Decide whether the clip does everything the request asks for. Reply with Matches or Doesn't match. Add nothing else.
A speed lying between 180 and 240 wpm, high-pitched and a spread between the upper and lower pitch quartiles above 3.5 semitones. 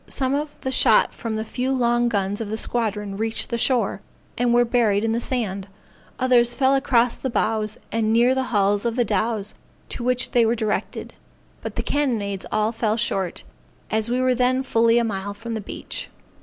Doesn't match